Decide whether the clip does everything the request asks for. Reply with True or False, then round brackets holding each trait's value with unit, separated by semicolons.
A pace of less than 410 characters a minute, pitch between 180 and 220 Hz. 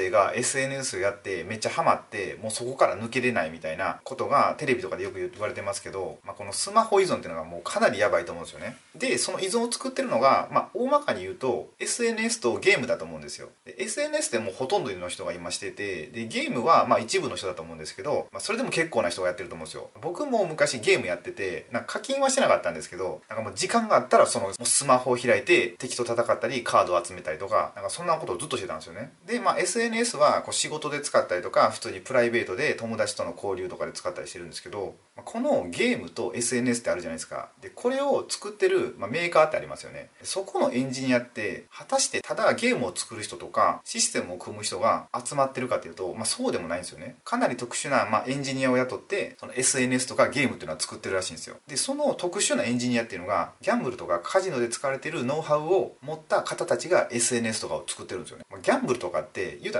False (530 characters per minute; 190 Hz)